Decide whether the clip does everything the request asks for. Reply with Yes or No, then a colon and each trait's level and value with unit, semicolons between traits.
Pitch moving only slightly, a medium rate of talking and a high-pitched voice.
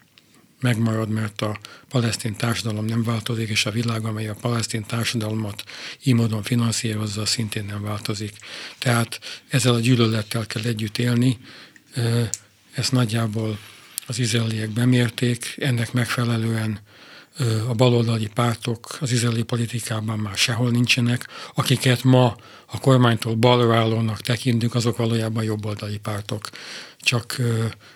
No: narrow, 1.8 semitones; average, 120 wpm; low, 115 Hz